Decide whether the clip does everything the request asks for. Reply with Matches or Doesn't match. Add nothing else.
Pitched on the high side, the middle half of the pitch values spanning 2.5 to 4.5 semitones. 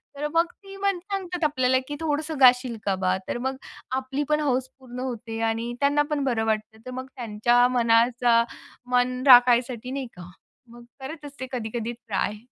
Matches